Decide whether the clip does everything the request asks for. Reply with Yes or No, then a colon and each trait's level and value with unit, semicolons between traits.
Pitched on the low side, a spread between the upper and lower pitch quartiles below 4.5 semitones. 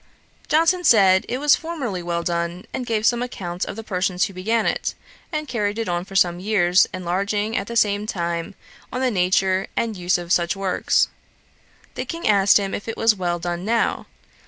No: high, 195 Hz; average, 4.1 semitones